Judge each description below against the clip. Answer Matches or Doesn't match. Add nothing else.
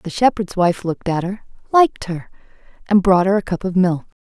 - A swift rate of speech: Matches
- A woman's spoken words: Matches